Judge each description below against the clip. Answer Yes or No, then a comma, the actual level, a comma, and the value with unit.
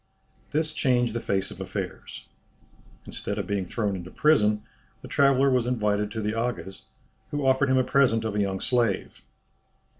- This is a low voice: Yes, low, 115 Hz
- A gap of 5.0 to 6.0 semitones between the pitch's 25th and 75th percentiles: No, average, 4.3 semitones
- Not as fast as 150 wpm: No, average, 170 wpm